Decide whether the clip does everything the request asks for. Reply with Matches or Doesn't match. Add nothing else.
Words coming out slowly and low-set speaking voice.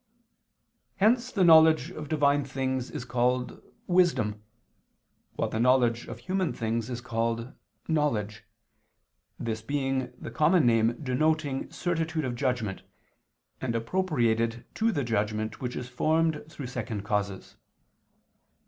Matches